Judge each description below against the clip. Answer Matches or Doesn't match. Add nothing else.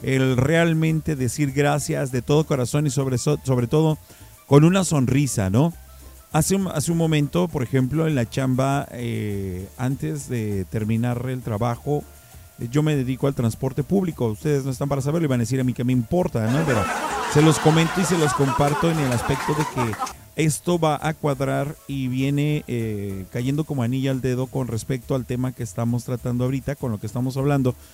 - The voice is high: Doesn't match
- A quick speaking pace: Matches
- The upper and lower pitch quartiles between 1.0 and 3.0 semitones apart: Doesn't match